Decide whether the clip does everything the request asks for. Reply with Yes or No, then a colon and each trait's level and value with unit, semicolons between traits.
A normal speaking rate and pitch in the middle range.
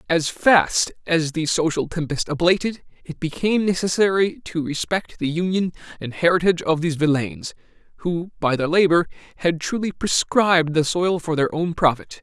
Yes: average, 155 wpm; medium, 170 Hz